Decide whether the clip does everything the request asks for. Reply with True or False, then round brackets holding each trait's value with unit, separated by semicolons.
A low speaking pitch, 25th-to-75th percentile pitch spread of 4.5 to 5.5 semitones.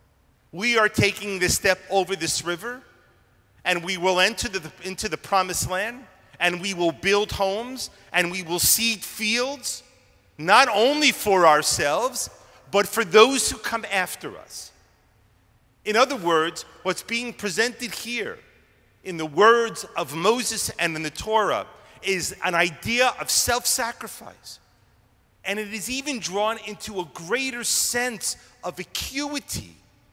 False (195 Hz; 4.9 semitones)